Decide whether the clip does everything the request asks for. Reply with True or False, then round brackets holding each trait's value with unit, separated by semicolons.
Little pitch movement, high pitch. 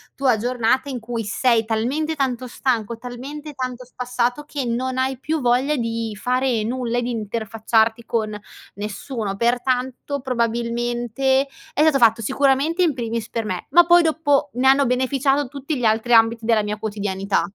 False (3.0 semitones; 245 Hz)